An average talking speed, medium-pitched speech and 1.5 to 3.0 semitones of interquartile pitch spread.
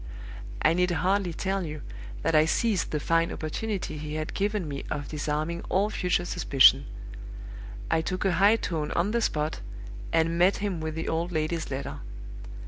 No: average, 170 wpm; medium, 165 Hz; average, 3.4 semitones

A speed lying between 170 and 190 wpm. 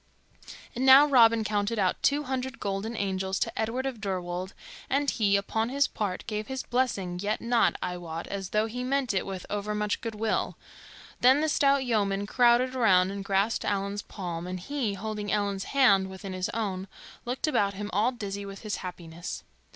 Yes: average, 180 wpm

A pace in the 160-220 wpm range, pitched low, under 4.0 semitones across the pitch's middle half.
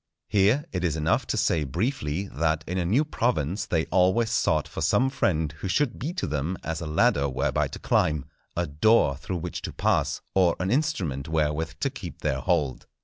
No: average, 200 wpm; very low, 85 Hz; average, 5.3 semitones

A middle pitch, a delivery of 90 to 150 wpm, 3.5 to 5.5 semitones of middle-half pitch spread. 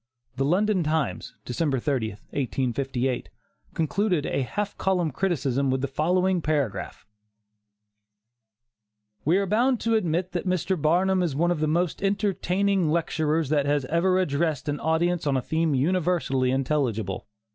Yes: medium, 160 Hz; slow, 135 wpm; average, 4.8 semitones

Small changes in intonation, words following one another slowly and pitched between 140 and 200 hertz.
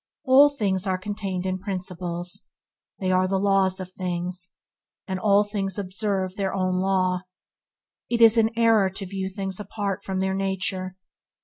No: narrow, 1.5 semitones; average, 155 wpm; high, 190 Hz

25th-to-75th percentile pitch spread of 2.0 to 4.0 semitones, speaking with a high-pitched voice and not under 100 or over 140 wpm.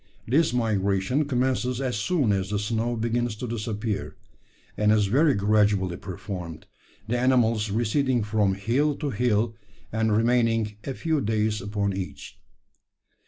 No: average, 3.2 semitones; low, 110 Hz; slow, 135 wpm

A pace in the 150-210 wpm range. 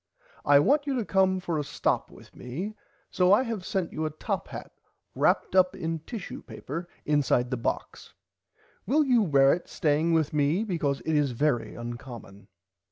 Yes: average, 175 wpm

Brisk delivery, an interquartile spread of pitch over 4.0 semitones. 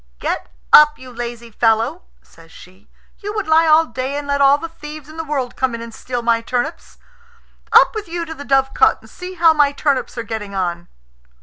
Yes: fast, 210 wpm; average, 5.3 semitones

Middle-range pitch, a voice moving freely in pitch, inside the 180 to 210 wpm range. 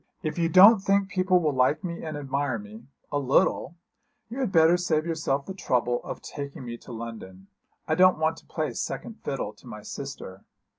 Yes: medium, 150 Hz; wide, 6.1 semitones; average, 195 wpm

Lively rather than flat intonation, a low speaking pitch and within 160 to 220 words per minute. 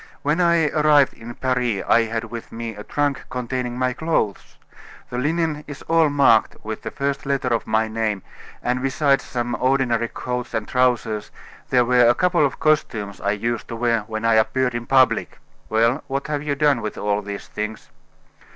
No: average, 3.6 semitones; low, 125 Hz; average, 185 wpm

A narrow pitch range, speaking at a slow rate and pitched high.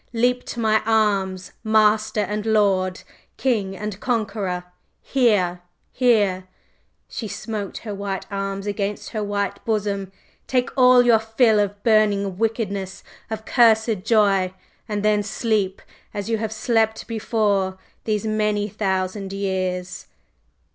Yes: narrow, 2.1 semitones; slow, 125 wpm; high, 210 Hz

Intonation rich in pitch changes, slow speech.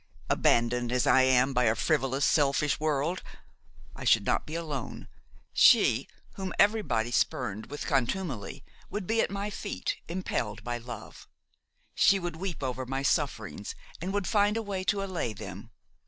No: wide, 7.4 semitones; average, 155 wpm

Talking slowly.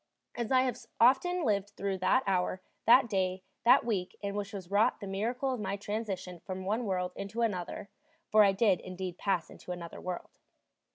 No: average, 190 wpm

